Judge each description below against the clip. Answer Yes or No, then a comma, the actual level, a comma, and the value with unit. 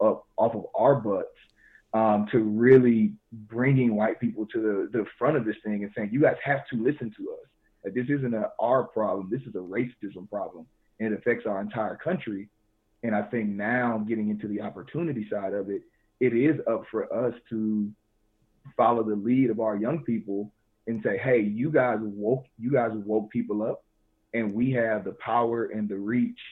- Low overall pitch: Yes, low, 110 Hz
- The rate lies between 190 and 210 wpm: Yes, average, 195 wpm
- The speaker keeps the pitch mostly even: Yes, narrow, 2.2 semitones